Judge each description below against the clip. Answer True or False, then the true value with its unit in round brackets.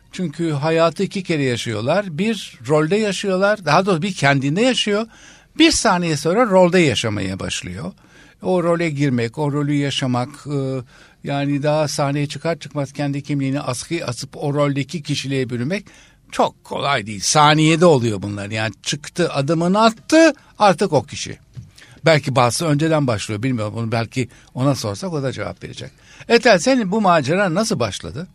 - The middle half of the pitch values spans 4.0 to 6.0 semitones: True (5.3 semitones)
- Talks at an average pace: False (150 wpm)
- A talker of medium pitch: True (145 Hz)